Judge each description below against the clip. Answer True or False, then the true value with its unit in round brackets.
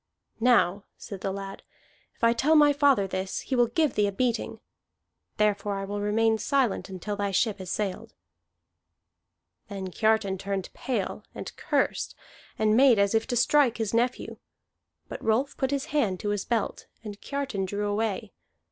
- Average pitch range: True (3.6 semitones)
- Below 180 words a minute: True (165 wpm)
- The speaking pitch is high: True (215 Hz)